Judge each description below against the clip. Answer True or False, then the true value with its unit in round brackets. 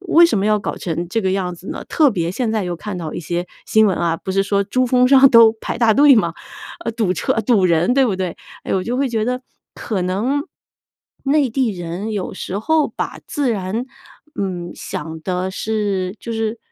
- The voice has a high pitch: True (210 Hz)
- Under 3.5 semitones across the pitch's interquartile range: False (4.8 semitones)